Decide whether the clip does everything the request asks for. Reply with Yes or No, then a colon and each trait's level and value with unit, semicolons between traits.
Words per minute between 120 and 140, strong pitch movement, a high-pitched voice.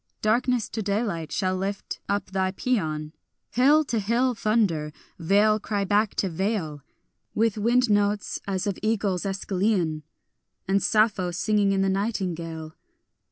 No: slow, 135 wpm; average, 2.8 semitones; high, 200 Hz